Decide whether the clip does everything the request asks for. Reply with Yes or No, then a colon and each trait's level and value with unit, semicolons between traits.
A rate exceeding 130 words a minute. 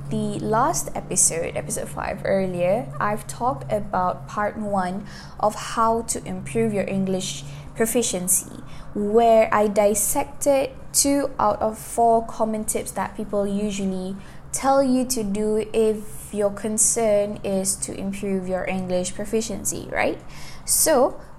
No: average, 125 wpm